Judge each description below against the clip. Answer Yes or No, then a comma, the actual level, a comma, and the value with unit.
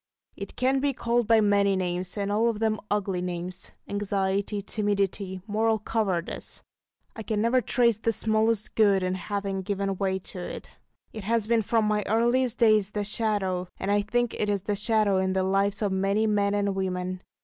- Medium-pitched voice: No, high, 205 Hz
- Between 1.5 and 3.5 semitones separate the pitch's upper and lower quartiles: Yes, narrow, 2.4 semitones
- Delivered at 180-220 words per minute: Yes, average, 185 wpm